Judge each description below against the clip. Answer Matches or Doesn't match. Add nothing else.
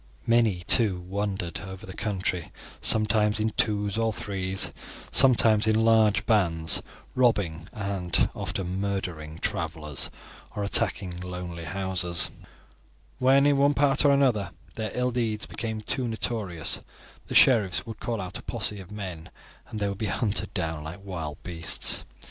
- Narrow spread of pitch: Doesn't match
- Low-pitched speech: Matches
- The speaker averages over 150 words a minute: Doesn't match